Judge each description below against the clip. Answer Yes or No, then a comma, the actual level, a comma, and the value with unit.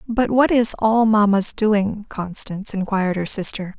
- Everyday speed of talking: Yes, average, 160 wpm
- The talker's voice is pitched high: Yes, high, 210 Hz